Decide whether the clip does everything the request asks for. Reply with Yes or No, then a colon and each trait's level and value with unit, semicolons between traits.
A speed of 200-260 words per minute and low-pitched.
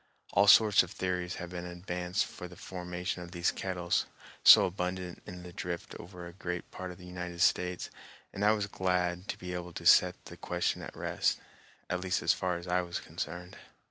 Yes: fast, 205 wpm; very low, 90 Hz